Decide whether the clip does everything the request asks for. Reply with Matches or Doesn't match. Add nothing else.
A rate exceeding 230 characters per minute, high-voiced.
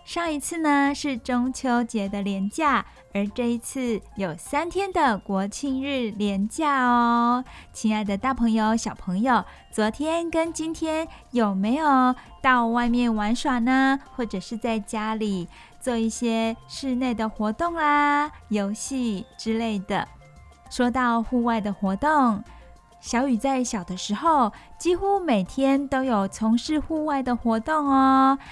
Doesn't match